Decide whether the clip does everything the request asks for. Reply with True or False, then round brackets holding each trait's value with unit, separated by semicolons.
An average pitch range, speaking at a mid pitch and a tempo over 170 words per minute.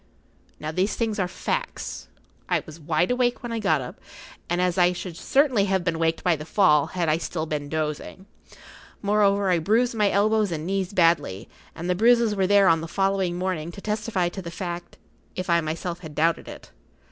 True (3.6 semitones; 180 Hz; 200 wpm)